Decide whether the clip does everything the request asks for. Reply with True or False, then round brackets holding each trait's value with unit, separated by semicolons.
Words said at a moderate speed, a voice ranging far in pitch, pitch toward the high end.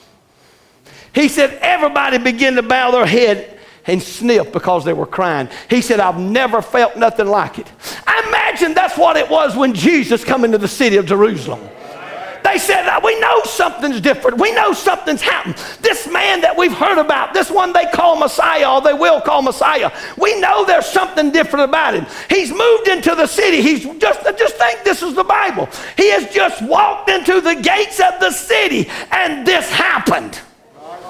True (185 wpm; 7.4 semitones; 310 Hz)